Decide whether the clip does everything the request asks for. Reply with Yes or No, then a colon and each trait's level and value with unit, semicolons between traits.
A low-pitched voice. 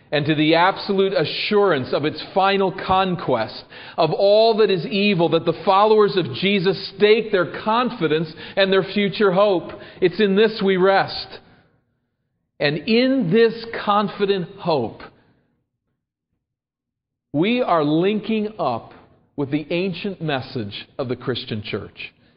No: high, 190 Hz